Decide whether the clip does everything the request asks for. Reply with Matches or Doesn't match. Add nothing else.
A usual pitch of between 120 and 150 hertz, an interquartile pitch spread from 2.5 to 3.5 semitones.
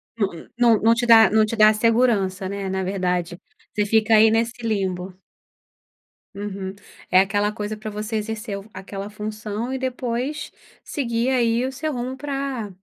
Doesn't match